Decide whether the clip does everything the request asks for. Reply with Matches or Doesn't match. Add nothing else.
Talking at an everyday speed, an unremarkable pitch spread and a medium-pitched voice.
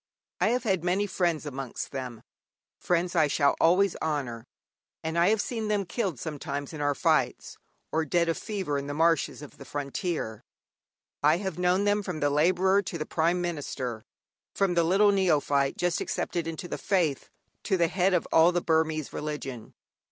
Matches